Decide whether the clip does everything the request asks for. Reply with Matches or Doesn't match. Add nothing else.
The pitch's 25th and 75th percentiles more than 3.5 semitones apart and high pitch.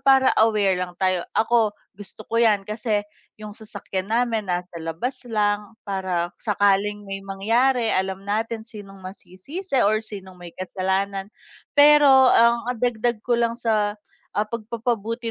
Doesn't match